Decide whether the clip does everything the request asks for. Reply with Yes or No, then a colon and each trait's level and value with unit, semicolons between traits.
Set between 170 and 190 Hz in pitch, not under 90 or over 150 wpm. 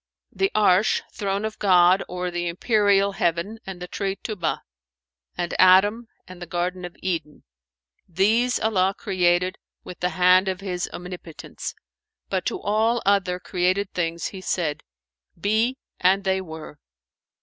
Yes: medium, 185 Hz; average, 140 wpm